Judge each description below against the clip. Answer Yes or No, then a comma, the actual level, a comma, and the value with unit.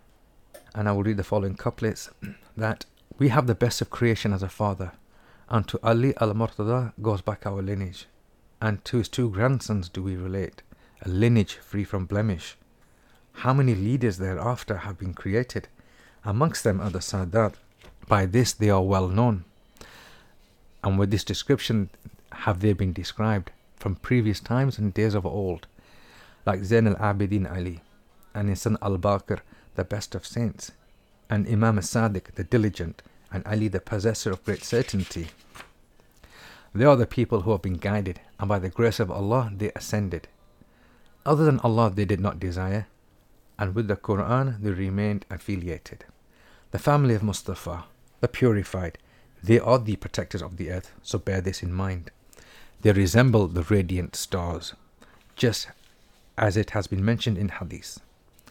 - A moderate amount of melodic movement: Yes, average, 3.0 semitones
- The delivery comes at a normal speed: Yes, average, 160 wpm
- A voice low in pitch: Yes, low, 105 Hz